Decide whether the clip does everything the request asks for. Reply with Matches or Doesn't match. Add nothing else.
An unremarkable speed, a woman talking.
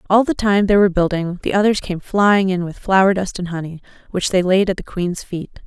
Doesn't match